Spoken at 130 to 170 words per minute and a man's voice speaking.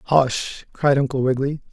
Yes: average, 140 wpm; male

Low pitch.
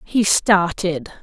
No: medium, 185 Hz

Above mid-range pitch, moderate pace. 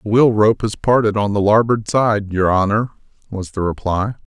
No: low, 105 Hz; average, 195 wpm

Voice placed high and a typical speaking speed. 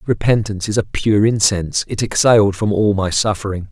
No: low, 105 Hz; average, 180 wpm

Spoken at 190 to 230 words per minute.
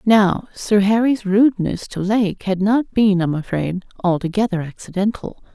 No: average, 150 wpm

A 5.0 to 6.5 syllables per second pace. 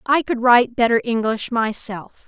No: 4.7 syllables/s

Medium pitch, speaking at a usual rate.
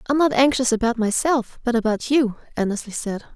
No: high, 240 Hz; average, 180 wpm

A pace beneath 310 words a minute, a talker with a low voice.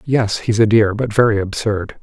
Yes: fast, 205 wpm; low, 110 Hz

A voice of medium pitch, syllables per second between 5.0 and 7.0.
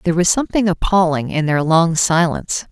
Yes: medium, 170 Hz; 5.9 syllables/s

